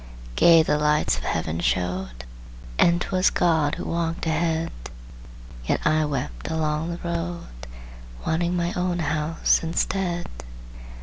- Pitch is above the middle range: No, medium, 160 Hz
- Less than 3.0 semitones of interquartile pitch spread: Yes, narrow, 2.6 semitones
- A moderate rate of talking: No, slow, 125 wpm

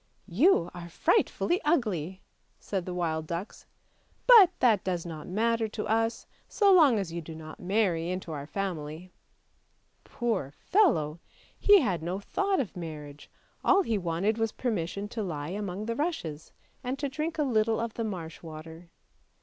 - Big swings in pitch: Yes, wide, 5.9 semitones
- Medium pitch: No, high, 195 Hz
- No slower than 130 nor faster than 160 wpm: No, average, 170 wpm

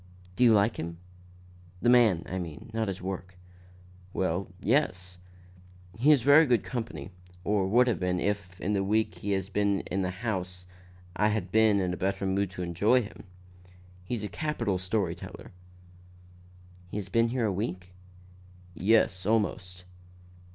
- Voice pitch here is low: Yes, low, 100 Hz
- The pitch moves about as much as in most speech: Yes, average, 3.5 semitones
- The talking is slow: No, average, 160 wpm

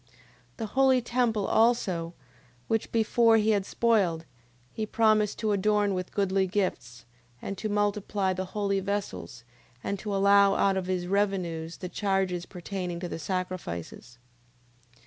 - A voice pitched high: Yes, high, 195 Hz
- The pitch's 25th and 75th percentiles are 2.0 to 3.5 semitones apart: Yes, average, 2.7 semitones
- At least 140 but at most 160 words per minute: Yes, average, 145 wpm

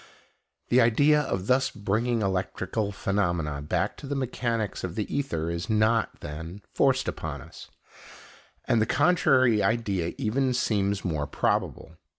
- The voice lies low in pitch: Yes, low, 105 Hz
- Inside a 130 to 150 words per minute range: Yes, average, 140 wpm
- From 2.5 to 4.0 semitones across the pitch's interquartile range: No, average, 5.0 semitones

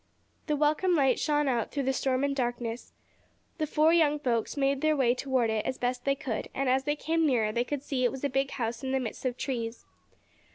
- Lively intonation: No, average, 3.1 semitones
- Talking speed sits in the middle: No, fast, 240 wpm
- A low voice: No, very high, 265 Hz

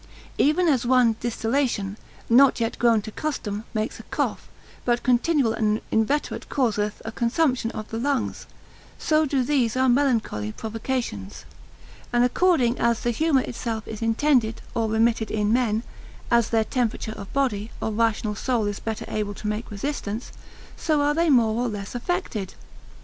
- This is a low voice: No, high, 235 Hz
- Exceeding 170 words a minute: No, average, 160 wpm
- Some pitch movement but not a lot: Yes, average, 3.3 semitones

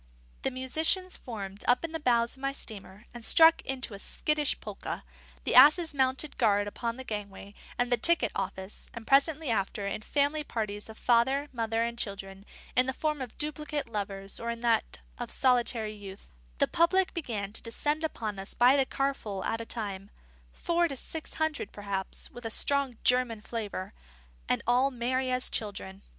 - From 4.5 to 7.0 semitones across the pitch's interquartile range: Yes, average, 5.0 semitones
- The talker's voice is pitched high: Yes, high, 240 Hz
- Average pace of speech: Yes, average, 180 wpm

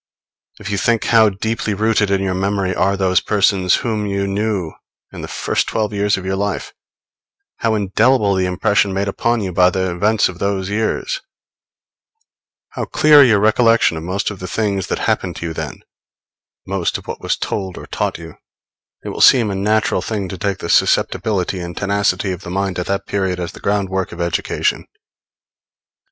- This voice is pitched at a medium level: No, low, 100 Hz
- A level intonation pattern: Yes, narrow, 2.2 semitones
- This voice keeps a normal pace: Yes, average, 190 wpm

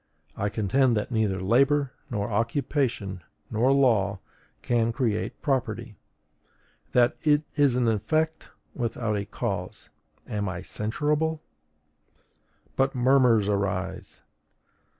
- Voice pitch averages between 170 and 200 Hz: No, low, 115 Hz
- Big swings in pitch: No, average, 4.7 semitones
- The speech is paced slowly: Yes, slow, 105 wpm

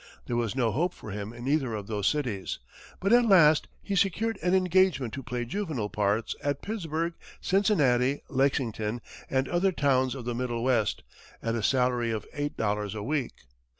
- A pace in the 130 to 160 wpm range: No, average, 180 wpm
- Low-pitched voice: Yes, low, 130 Hz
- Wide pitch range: Yes, wide, 6.1 semitones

